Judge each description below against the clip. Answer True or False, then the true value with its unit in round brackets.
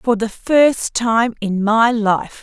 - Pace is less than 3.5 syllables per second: True (3.0 syllables/s)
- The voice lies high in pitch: True (225 Hz)